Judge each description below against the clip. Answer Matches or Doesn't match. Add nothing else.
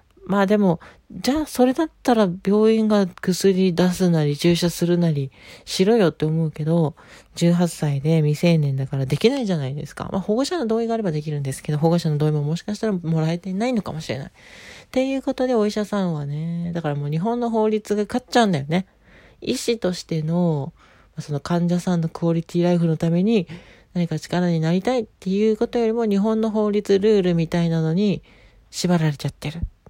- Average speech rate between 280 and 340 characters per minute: Doesn't match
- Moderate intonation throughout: Matches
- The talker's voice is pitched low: Doesn't match